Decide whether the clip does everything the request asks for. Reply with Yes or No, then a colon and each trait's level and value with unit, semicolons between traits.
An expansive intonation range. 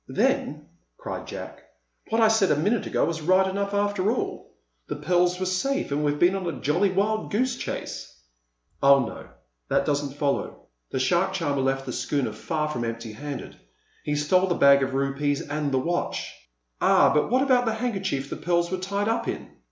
Yes: wide, 6.0 semitones